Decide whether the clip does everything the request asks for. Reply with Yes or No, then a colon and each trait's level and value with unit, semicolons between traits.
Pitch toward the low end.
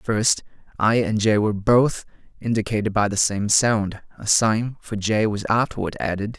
Yes: low, 110 Hz